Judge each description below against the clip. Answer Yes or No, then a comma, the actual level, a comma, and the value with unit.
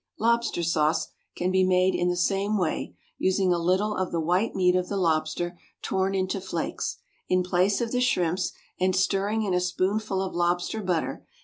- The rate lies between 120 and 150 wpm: No, average, 185 wpm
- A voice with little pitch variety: Yes, narrow, 1.8 semitones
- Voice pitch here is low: No, medium, 185 Hz